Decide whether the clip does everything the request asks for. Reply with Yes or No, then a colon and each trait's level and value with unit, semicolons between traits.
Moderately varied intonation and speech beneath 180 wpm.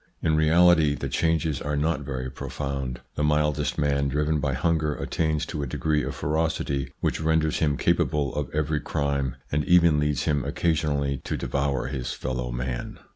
No: narrow, 2.1 semitones; average, 170 wpm